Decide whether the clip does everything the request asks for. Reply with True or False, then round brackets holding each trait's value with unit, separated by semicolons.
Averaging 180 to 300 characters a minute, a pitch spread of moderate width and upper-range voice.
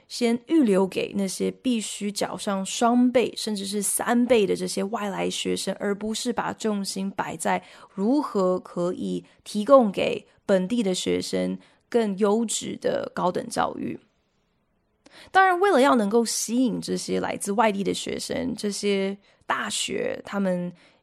True (215 characters per minute; 4.4 semitones; 205 Hz)